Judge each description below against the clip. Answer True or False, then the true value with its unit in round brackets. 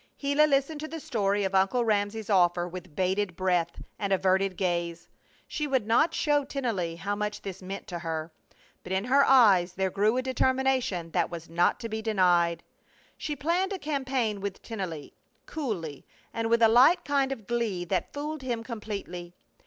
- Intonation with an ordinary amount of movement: False (6.4 semitones)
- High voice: True (205 Hz)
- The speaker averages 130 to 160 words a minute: False (175 wpm)